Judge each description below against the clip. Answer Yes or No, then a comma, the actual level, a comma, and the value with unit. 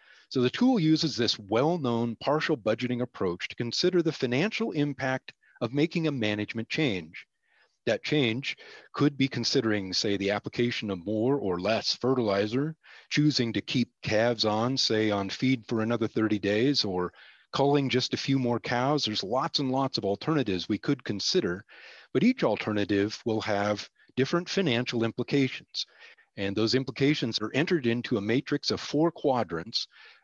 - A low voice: Yes, low, 125 Hz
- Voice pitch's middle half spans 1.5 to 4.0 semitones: No, average, 4.9 semitones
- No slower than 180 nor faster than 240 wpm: No, average, 160 wpm